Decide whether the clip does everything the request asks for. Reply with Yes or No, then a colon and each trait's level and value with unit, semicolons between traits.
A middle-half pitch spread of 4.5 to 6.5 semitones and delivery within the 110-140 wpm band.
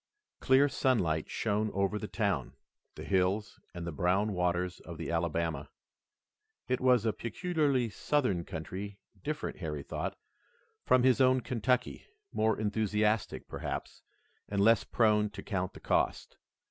Yes: average, 5.3 semitones; slow, 135 wpm